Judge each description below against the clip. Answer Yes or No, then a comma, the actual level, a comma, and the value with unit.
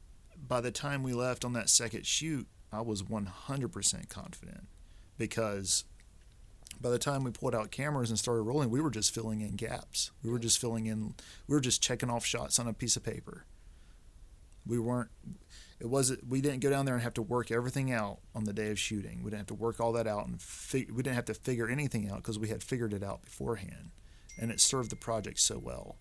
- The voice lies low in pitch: Yes, low, 115 Hz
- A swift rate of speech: Yes, fast, 225 wpm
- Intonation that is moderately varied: Yes, average, 3.2 semitones